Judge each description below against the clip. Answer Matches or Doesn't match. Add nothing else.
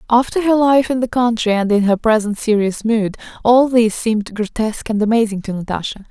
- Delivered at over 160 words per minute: Matches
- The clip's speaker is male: Doesn't match